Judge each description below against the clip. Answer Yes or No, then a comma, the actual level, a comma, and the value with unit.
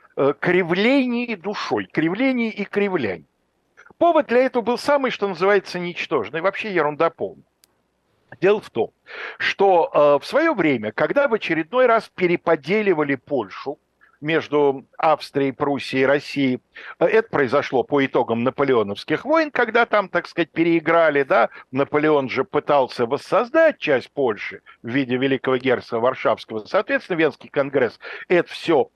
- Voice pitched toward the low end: No, medium, 165 Hz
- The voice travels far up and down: Yes, wide, 7.7 semitones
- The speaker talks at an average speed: Yes, average, 130 wpm